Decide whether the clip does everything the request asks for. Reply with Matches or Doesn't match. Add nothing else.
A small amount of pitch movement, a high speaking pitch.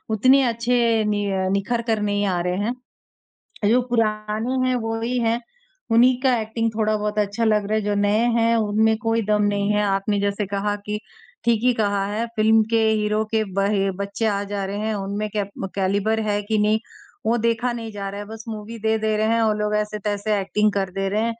Matches